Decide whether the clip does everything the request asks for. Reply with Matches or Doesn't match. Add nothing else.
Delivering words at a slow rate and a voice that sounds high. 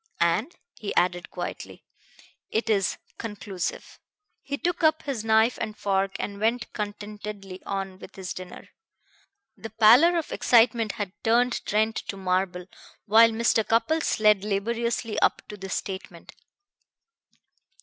Matches